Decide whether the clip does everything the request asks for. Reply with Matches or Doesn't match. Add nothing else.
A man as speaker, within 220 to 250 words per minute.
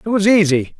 Matches